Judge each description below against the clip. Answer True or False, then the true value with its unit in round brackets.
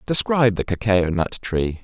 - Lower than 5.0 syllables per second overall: True (4.8 syllables/s)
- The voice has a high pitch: False (105 Hz)